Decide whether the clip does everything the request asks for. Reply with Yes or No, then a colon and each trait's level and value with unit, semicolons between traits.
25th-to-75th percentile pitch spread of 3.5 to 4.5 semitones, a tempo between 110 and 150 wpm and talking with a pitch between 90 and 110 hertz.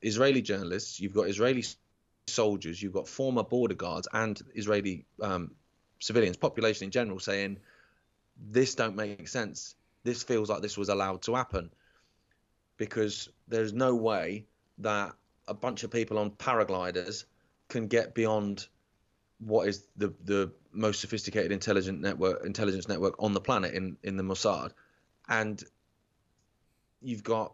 No: narrow, 2.5 semitones; average, 140 wpm; low, 105 Hz